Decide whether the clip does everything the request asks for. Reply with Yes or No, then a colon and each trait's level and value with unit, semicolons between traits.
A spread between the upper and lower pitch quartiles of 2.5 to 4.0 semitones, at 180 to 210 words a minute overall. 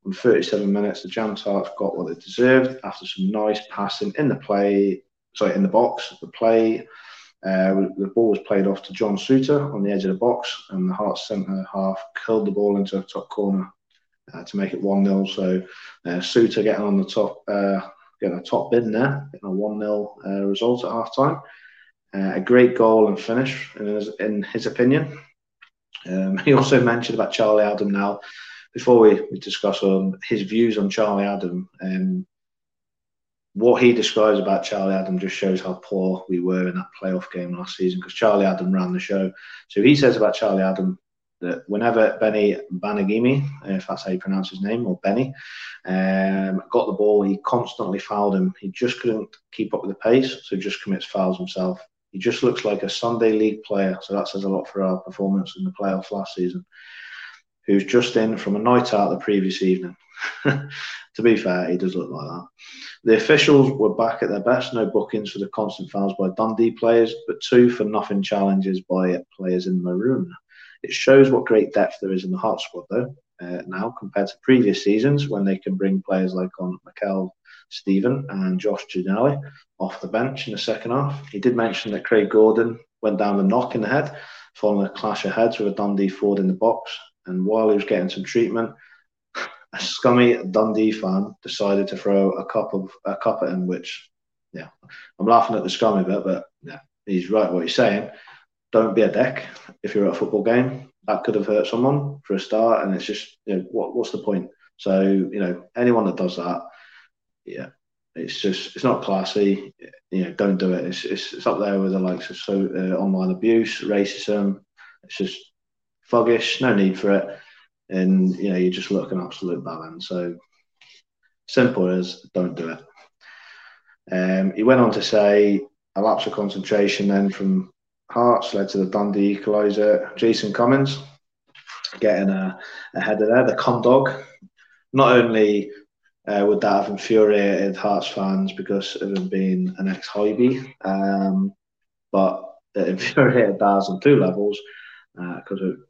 Yes: average, 3.2 semitones; average, 190 wpm